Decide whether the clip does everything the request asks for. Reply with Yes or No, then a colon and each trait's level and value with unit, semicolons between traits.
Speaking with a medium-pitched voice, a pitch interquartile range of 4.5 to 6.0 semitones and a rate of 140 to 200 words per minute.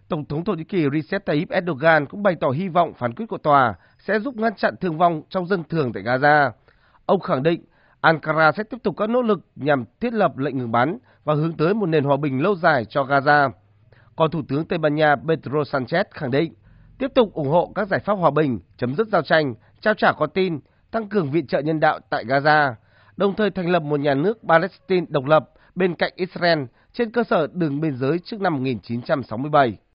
No: medium, 155 Hz; average, 5.1 semitones; average, 225 wpm